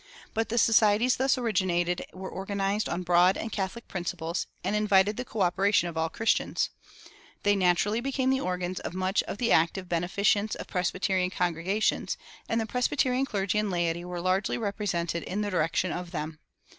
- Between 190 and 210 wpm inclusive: No, average, 170 wpm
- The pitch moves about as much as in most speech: Yes, average, 3.3 semitones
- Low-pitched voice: No, high, 190 Hz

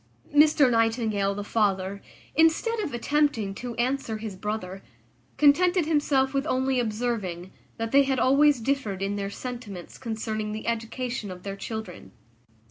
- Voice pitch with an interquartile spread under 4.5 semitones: No, average, 5.2 semitones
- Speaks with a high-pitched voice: Yes, high, 230 Hz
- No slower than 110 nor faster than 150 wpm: Yes, average, 140 wpm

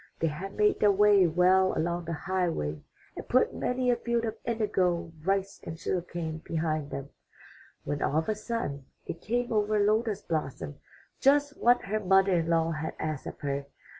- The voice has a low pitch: No, medium, 185 Hz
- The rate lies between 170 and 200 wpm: Yes, average, 180 wpm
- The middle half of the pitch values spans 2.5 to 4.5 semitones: No, average, 5.0 semitones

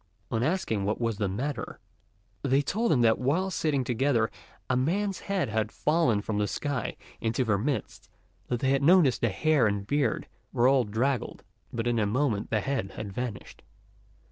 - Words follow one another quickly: No, average, 180 wpm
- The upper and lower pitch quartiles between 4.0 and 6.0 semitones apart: Yes, average, 4.6 semitones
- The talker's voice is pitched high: No, low, 125 Hz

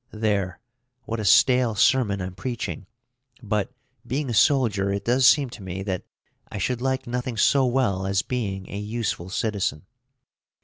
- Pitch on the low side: Yes, low, 110 Hz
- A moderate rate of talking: Yes, average, 160 wpm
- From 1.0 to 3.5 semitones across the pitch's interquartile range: No, average, 4.2 semitones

